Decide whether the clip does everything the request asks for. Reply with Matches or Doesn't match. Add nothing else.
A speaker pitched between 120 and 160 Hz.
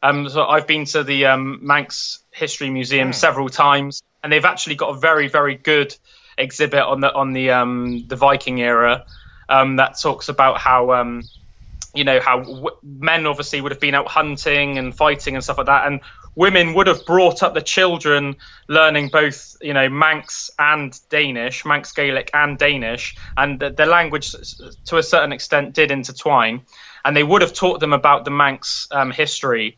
Matches